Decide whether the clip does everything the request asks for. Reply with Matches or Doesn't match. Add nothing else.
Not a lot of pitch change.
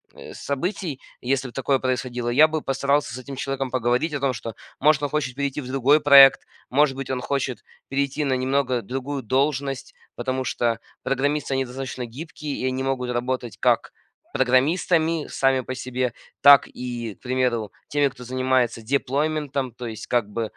Matches